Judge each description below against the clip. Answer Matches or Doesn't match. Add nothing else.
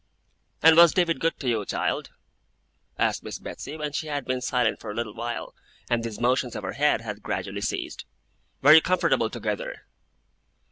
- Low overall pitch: Matches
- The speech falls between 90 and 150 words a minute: Doesn't match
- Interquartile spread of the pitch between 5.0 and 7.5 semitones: Matches